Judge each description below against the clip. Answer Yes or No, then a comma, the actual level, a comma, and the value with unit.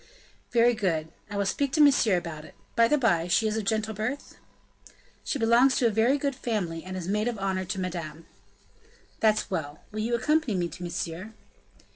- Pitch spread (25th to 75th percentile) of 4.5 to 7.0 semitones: Yes, average, 4.9 semitones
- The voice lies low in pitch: No, high, 215 Hz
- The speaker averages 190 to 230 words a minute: Yes, average, 195 wpm